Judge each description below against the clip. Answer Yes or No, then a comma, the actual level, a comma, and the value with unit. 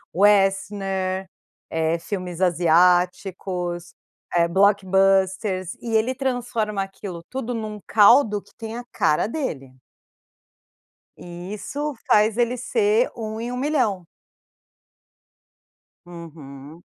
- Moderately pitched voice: No, high, 195 Hz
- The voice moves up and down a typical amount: Yes, average, 4.2 semitones